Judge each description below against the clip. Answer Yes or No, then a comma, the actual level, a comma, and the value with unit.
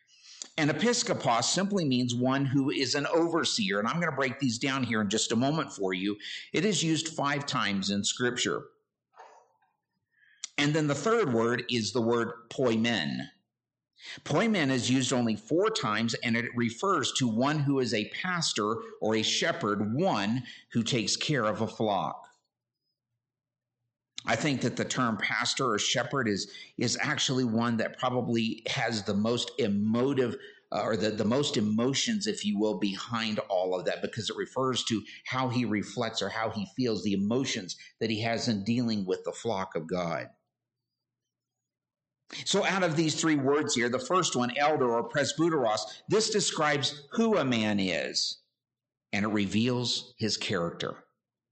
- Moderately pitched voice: No, low, 125 Hz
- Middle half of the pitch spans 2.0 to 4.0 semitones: No, average, 4.5 semitones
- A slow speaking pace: No, average, 165 wpm